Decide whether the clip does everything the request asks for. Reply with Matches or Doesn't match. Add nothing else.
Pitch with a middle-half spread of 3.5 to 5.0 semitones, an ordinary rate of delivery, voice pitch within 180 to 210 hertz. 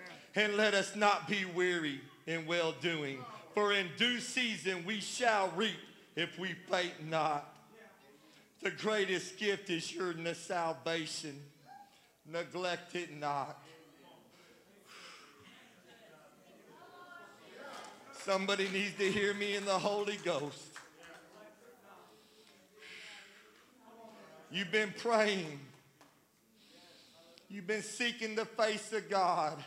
Doesn't match